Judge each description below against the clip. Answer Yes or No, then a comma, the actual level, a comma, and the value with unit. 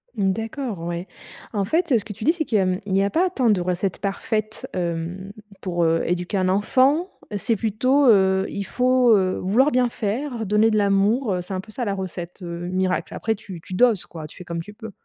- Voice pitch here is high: Yes, high, 200 Hz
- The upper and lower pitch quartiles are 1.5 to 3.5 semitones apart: No, average, 4.0 semitones